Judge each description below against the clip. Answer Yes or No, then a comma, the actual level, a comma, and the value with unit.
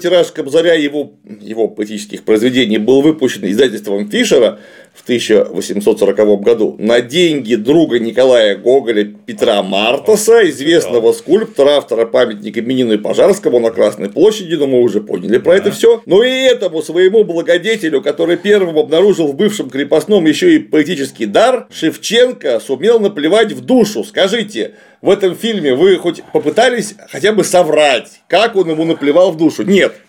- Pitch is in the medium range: Yes, medium, 175 Hz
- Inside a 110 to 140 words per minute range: No, average, 150 wpm